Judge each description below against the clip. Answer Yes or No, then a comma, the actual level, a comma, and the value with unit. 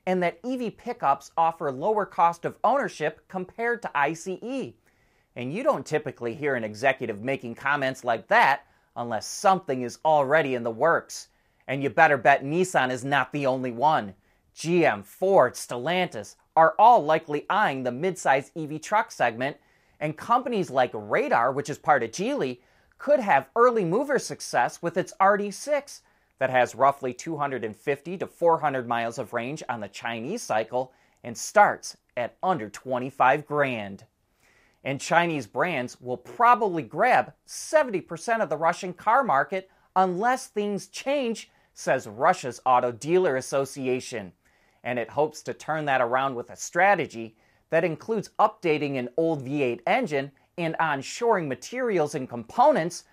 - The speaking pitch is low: No, medium, 150 Hz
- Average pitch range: No, wide, 6.5 semitones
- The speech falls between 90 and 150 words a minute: Yes, average, 145 wpm